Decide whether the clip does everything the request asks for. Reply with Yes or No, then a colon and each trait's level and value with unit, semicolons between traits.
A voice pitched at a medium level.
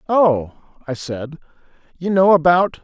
Yes: medium, 165 Hz